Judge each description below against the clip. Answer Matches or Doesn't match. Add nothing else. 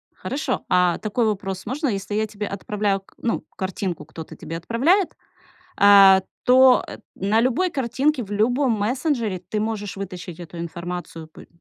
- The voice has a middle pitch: Doesn't match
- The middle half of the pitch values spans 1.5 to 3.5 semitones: Doesn't match